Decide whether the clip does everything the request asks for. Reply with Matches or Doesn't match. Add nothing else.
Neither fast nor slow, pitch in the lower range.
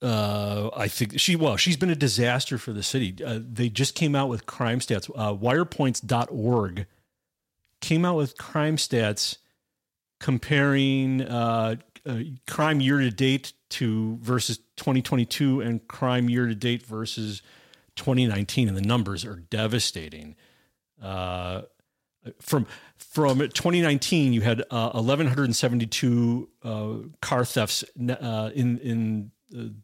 Doesn't match